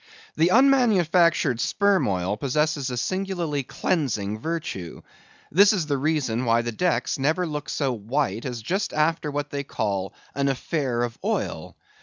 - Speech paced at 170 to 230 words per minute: No, average, 150 wpm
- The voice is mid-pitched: Yes, medium, 145 Hz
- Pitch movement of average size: No, wide, 6.1 semitones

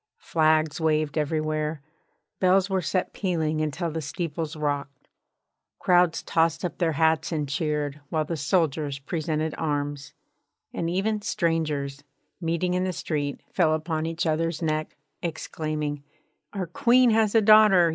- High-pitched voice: No, medium, 160 Hz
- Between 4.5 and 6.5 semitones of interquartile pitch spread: No, narrow, 2.6 semitones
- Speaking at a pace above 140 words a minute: No, slow, 135 wpm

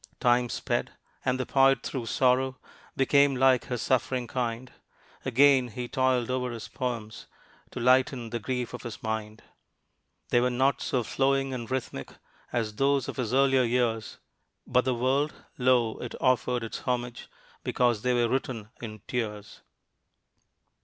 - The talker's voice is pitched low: Yes, low, 125 Hz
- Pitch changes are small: Yes, narrow, 1.9 semitones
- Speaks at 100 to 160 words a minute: Yes, average, 150 wpm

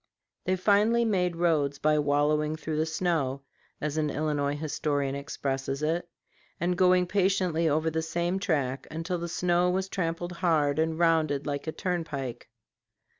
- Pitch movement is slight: No, average, 3.3 semitones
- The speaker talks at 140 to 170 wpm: Yes, average, 150 wpm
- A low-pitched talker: No, medium, 160 Hz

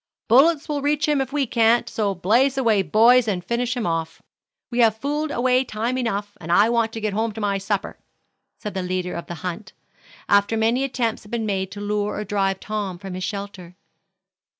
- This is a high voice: Yes, high, 215 Hz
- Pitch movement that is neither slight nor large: Yes, average, 3.8 semitones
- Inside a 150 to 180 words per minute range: No, average, 200 wpm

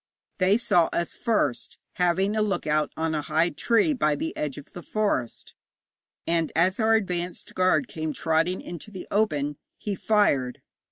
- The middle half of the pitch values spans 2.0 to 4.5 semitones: No, average, 4.9 semitones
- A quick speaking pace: No, average, 165 wpm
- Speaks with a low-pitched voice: No, medium, 175 Hz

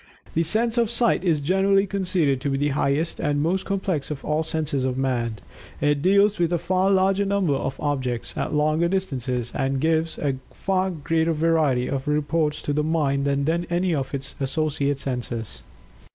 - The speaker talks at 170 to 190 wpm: Yes, average, 180 wpm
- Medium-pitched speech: Yes, medium, 155 Hz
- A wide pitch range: No, average, 4.7 semitones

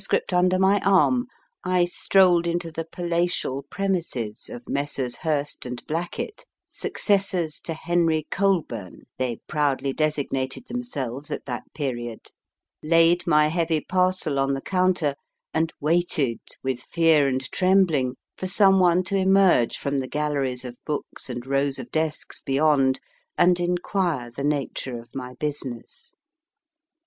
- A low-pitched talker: No, medium, 155 Hz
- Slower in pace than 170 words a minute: Yes, slow, 135 wpm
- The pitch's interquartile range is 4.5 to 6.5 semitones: Yes, average, 4.9 semitones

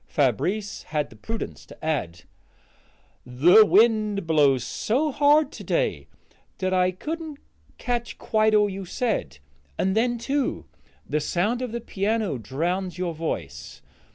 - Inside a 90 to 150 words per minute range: Yes, slow, 135 wpm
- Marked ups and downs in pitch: Yes, wide, 6.9 semitones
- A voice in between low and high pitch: No, high, 200 Hz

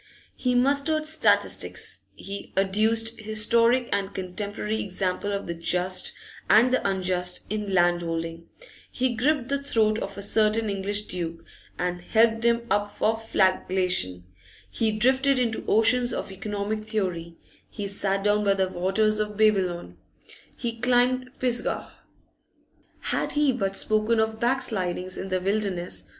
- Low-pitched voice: No, high, 210 Hz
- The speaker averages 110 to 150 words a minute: Yes, slow, 135 wpm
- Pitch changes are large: No, average, 3.6 semitones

